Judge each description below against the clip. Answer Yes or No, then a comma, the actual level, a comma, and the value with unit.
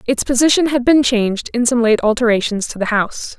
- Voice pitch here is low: No, high, 235 Hz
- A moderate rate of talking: No, fast, 215 wpm